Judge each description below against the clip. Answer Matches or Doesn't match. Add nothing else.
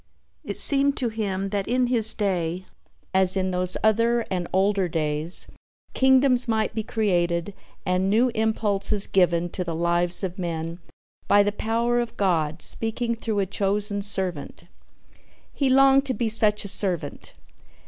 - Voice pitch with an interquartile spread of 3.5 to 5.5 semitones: Matches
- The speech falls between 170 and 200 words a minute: Doesn't match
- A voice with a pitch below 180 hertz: Doesn't match